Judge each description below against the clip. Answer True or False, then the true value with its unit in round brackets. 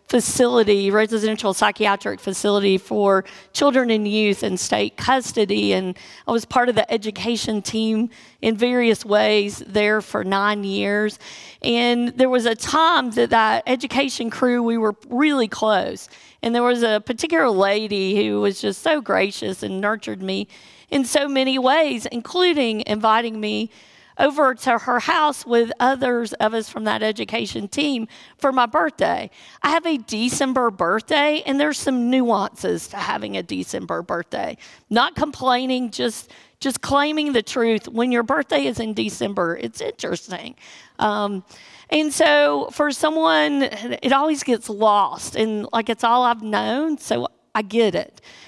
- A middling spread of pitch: True (3.9 semitones)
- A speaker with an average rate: True (150 wpm)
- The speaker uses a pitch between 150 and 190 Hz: False (230 Hz)